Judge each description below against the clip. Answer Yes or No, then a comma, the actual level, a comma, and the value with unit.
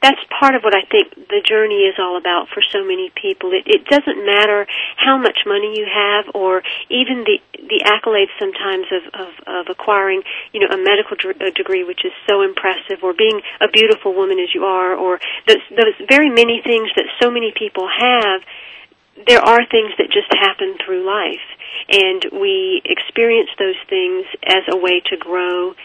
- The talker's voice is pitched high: Yes, very high, 285 Hz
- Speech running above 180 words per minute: Yes, average, 190 wpm